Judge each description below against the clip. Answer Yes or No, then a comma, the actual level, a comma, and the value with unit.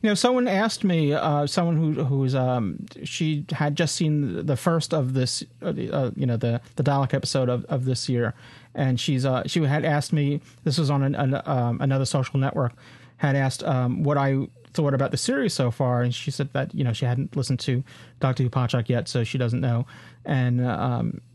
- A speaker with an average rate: No, fast, 210 wpm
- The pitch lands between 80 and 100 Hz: No, low, 135 Hz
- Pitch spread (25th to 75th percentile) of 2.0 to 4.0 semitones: Yes, average, 2.8 semitones